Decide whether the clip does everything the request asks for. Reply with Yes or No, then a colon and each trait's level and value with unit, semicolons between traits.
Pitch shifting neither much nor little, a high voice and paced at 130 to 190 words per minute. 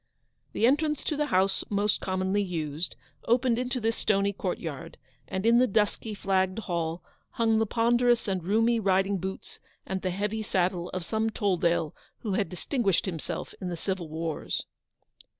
Yes: average, 3.7 semitones; high, 195 Hz; average, 160 wpm